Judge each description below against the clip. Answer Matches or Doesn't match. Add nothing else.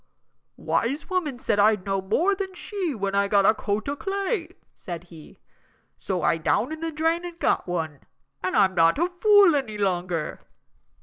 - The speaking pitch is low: Doesn't match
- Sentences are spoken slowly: Doesn't match